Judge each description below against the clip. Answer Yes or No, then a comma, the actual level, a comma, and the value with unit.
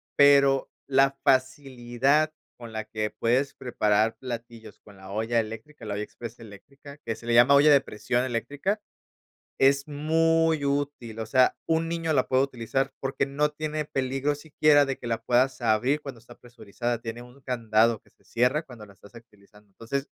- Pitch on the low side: Yes, low, 130 Hz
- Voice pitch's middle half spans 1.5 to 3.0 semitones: No, average, 3.7 semitones